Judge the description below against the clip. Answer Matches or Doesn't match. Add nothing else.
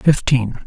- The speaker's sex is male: Matches